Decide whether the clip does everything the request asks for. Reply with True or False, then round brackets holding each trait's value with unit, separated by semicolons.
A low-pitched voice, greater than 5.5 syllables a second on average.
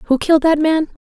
False (305 Hz; 5.8 syllables/s)